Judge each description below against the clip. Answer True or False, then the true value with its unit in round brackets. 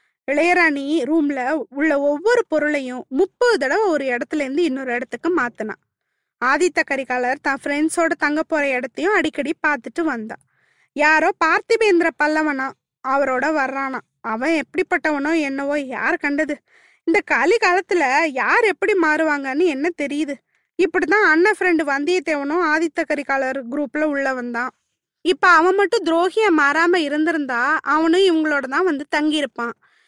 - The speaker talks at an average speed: True (120 wpm)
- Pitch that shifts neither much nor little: True (4.0 semitones)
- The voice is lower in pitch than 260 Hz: False (310 Hz)